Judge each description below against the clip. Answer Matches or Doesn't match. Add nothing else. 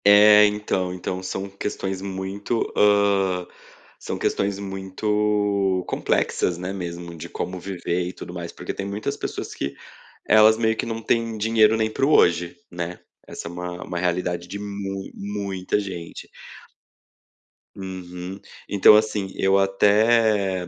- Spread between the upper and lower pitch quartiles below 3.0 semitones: Matches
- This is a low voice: Matches